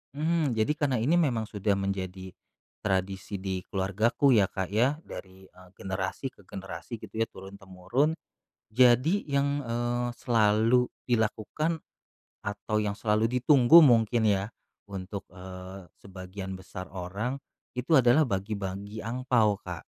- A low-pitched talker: Yes, low, 105 Hz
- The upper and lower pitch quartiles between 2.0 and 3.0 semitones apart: No, average, 4.5 semitones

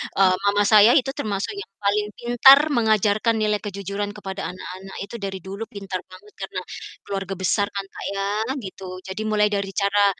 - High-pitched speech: Yes, high, 200 Hz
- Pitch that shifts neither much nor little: No, narrow, 1.6 semitones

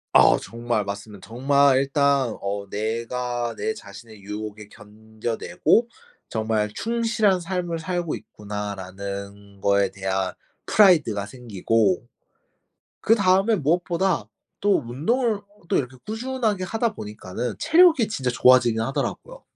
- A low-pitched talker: Yes, low, 120 Hz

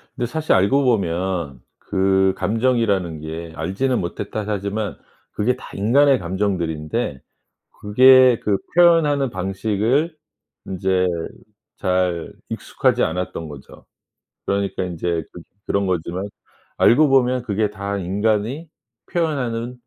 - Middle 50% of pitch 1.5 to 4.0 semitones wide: No, average, 5.3 semitones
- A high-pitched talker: No, low, 100 Hz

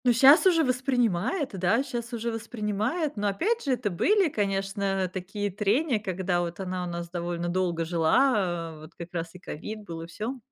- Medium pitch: No, high, 200 Hz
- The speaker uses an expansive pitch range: Yes, wide, 5.9 semitones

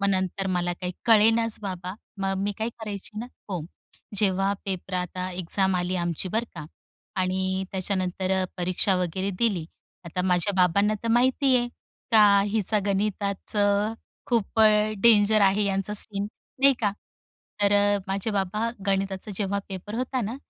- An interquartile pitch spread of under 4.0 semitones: Yes, narrow, 2.4 semitones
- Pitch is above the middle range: Yes, high, 195 Hz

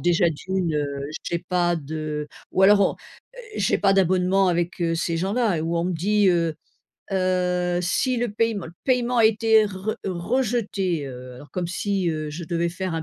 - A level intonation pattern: No, average, 3.3 semitones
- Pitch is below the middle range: No, medium, 180 Hz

